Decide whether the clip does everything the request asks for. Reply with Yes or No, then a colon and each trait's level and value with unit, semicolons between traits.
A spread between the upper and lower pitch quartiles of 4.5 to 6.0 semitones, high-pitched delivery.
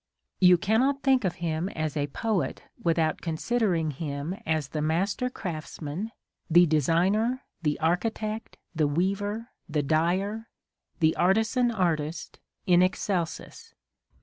No: average, 5.3 semitones; medium, 175 Hz